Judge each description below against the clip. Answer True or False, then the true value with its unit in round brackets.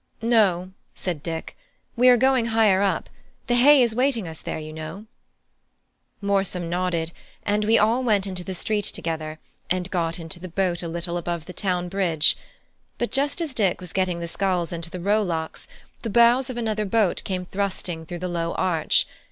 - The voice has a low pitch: False (185 Hz)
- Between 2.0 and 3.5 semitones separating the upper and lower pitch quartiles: False (4.3 semitones)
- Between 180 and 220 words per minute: True (185 wpm)